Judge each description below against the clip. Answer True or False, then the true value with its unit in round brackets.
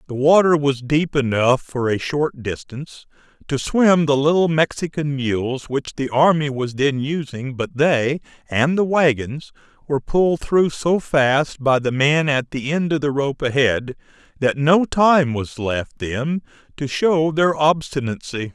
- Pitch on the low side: False (145 Hz)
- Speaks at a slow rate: False (165 wpm)